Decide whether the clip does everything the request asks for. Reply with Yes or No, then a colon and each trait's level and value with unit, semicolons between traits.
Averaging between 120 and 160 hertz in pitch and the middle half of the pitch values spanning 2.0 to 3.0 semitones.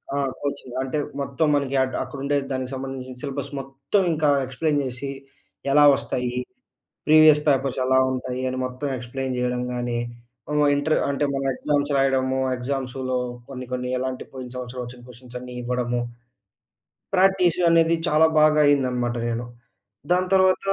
Yes: low, 135 Hz; narrow, 2.5 semitones